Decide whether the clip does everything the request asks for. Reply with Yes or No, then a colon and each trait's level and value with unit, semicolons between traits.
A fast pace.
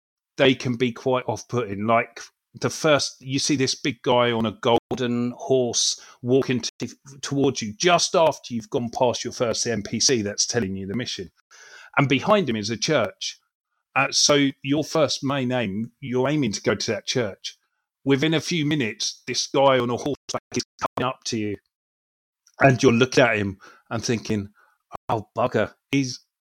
No: average, 175 wpm